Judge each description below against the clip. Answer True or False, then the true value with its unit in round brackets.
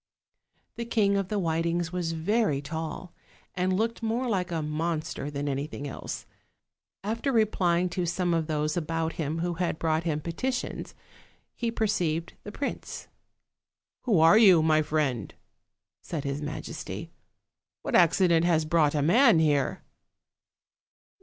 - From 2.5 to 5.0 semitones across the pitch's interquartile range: True (4.0 semitones)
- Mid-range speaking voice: True (170 Hz)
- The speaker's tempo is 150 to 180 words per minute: False (140 wpm)